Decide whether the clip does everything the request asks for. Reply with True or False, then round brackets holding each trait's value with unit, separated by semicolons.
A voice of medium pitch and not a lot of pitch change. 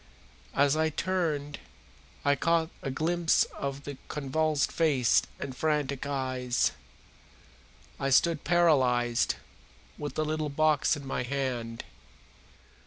False (145 Hz; 3.0 semitones)